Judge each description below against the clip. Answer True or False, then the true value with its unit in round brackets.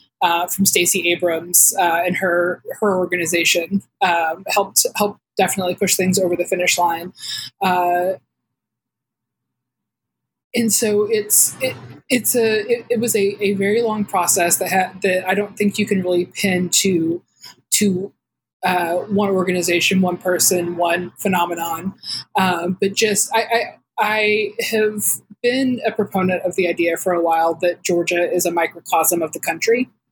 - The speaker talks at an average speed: True (155 wpm)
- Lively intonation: False (3.0 semitones)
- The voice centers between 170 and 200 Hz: True (185 Hz)